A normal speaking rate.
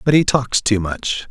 No: fast, 230 wpm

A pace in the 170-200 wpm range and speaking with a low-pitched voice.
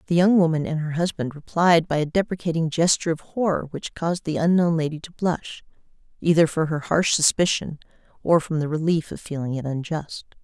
No: average, 190 wpm; medium, 160 Hz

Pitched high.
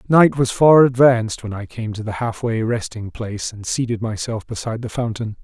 No: low, 115 Hz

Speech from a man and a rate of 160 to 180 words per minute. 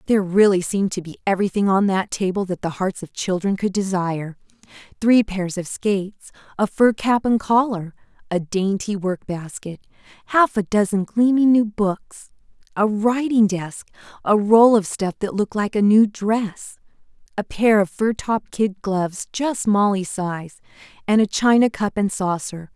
No: female; average, 165 wpm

